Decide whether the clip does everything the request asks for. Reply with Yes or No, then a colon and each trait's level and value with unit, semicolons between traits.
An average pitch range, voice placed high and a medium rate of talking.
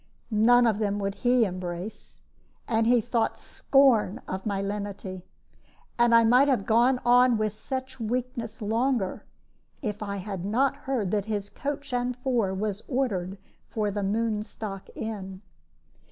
Yes: average, 3.5 semitones; high, 220 Hz; average, 145 wpm